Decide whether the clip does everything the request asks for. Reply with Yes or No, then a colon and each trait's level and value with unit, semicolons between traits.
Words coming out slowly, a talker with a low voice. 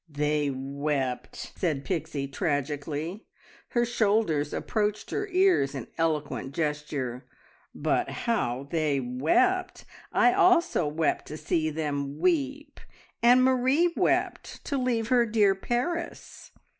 No: slow, 115 wpm; medium, 165 Hz